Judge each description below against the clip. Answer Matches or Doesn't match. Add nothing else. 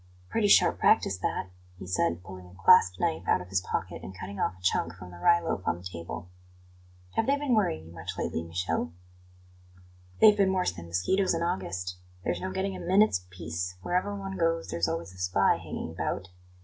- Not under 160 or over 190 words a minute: Doesn't match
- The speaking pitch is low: Matches